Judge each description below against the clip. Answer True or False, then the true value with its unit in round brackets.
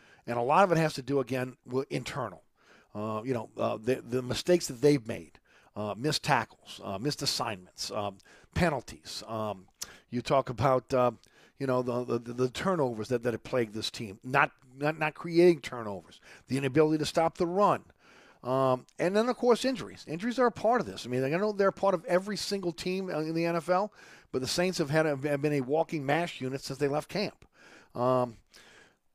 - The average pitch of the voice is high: False (135 Hz)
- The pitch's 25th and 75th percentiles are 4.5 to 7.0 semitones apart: True (5.5 semitones)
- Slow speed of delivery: False (205 wpm)